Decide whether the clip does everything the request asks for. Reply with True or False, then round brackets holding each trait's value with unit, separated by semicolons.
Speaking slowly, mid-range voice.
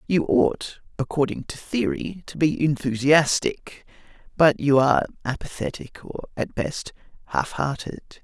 True (125 wpm; 150 Hz)